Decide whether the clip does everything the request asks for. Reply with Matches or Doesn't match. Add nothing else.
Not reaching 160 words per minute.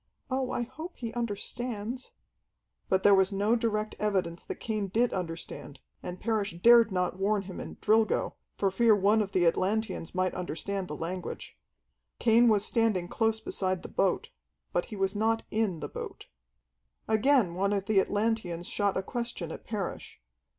Doesn't match